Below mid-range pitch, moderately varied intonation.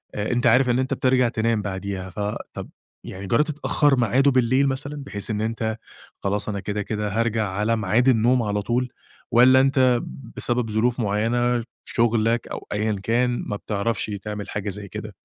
Yes: low, 115 Hz; average, 3.0 semitones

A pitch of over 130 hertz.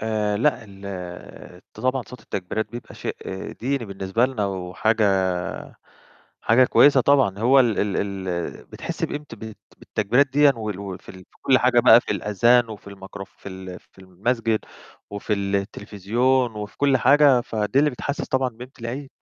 No: low, 110 Hz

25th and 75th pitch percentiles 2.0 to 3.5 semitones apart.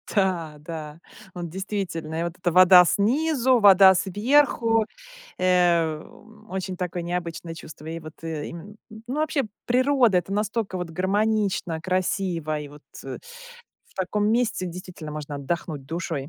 No: average, 4.2 semitones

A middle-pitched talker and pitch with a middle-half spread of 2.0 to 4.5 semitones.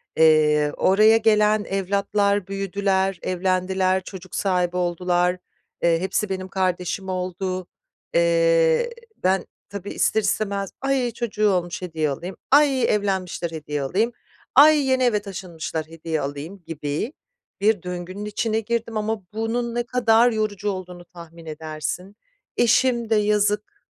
No: high, 195 Hz; average, 3.6 semitones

